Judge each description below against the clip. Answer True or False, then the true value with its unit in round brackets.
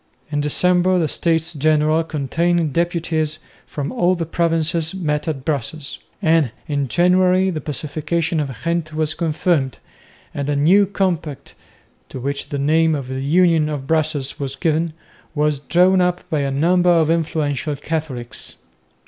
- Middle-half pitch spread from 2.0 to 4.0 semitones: True (2.8 semitones)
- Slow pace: False (150 wpm)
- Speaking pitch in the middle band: True (155 Hz)